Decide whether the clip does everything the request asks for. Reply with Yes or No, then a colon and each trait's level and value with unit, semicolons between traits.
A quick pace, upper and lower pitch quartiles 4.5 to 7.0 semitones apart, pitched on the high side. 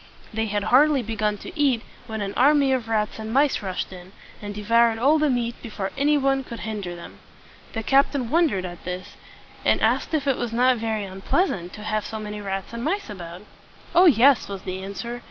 Yes: fast, 215 wpm; average, 4.9 semitones; high, 225 Hz